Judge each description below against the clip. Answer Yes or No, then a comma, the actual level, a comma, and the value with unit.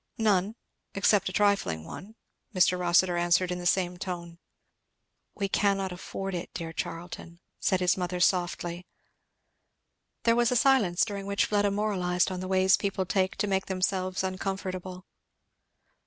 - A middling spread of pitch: No, narrow, 1.9 semitones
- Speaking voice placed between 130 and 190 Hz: Yes, medium, 185 Hz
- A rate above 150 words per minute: No, average, 145 wpm